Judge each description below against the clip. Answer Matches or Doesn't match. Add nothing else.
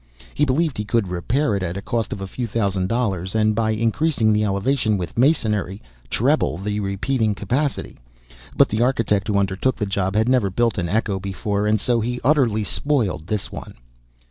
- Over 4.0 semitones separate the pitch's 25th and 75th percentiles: Doesn't match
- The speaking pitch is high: Doesn't match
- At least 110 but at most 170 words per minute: Doesn't match